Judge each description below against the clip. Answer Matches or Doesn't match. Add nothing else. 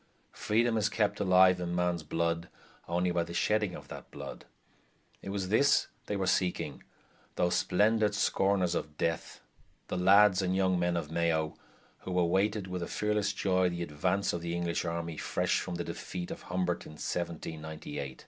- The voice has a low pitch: Matches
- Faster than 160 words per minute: Matches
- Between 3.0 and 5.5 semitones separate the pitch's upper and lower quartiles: Doesn't match